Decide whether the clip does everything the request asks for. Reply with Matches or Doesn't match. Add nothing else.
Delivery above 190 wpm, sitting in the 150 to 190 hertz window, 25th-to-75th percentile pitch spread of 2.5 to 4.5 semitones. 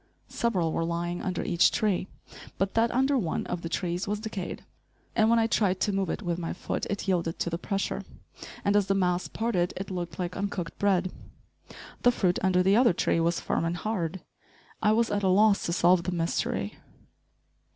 Matches